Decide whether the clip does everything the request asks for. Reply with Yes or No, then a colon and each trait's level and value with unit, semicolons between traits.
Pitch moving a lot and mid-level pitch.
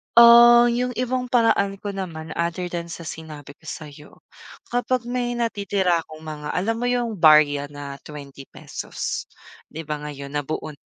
Yes: wide, 7.9 semitones; medium, 170 Hz